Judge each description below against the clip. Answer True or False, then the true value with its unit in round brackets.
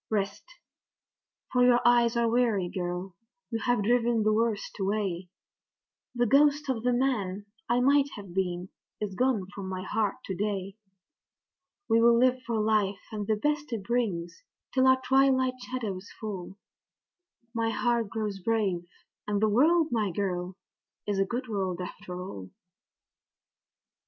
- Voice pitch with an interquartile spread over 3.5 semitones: True (4.1 semitones)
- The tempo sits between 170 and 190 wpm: False (145 wpm)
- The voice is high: True (215 Hz)